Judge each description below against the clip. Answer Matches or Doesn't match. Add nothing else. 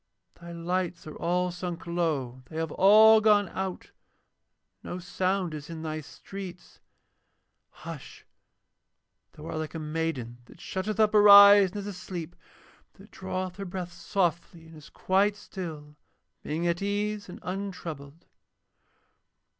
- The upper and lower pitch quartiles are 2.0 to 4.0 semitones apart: Matches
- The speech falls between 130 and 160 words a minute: Matches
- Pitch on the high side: Doesn't match